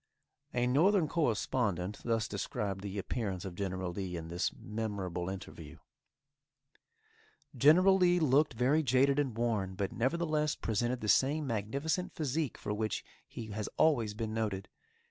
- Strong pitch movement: Yes, wide, 6.4 semitones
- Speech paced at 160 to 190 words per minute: No, average, 140 wpm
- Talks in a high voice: No, low, 115 Hz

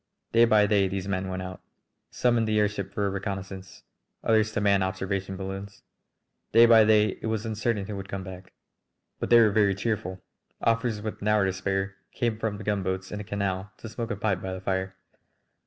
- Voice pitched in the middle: No, low, 100 Hz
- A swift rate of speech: Yes, fast, 210 wpm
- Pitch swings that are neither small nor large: No, narrow, 2.3 semitones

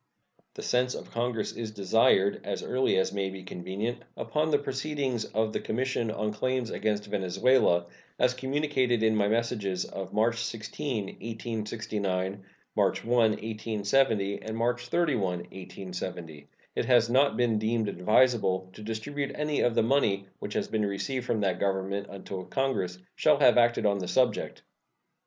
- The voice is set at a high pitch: No, low, 110 Hz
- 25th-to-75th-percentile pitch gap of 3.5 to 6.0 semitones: Yes, average, 4.0 semitones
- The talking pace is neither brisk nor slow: Yes, average, 155 wpm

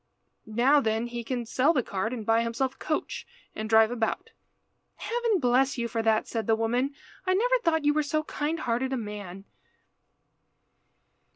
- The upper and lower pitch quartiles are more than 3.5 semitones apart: Yes, average, 4.7 semitones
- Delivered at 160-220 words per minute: Yes, average, 175 wpm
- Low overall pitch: No, high, 245 Hz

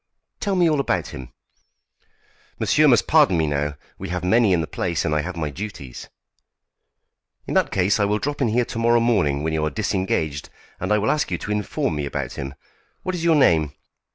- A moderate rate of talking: No, fast, 210 wpm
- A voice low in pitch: Yes, very low, 95 Hz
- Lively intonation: Yes, wide, 7.4 semitones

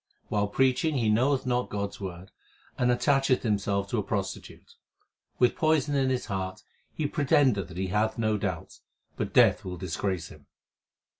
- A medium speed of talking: Yes, average, 165 wpm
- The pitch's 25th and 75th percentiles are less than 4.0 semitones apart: No, average, 5.1 semitones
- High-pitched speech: No, low, 110 Hz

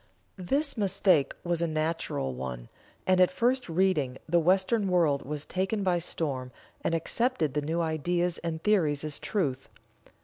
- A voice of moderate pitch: Yes, medium, 170 Hz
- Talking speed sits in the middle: Yes, average, 150 wpm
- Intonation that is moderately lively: Yes, average, 4.1 semitones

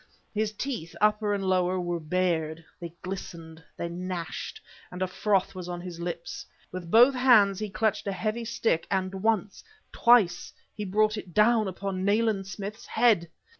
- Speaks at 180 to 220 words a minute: No, average, 170 wpm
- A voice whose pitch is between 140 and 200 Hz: Yes, high, 190 Hz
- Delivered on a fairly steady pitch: No, average, 3.4 semitones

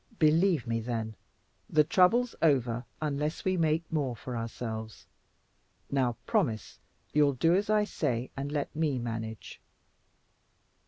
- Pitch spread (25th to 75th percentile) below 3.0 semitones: No, wide, 5.5 semitones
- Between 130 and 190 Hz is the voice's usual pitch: Yes, medium, 140 Hz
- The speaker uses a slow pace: Yes, slow, 125 wpm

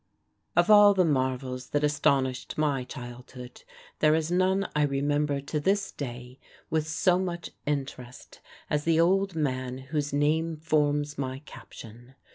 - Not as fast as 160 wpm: Yes, average, 140 wpm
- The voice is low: No, medium, 145 Hz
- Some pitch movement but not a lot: Yes, average, 3.6 semitones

